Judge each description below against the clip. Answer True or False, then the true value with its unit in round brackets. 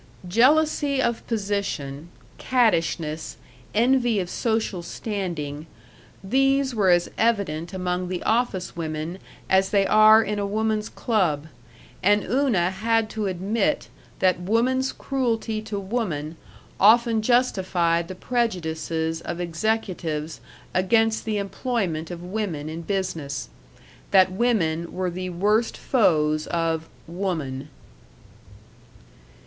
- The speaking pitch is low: False (190 Hz)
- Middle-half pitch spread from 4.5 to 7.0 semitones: True (4.9 semitones)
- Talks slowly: True (110 wpm)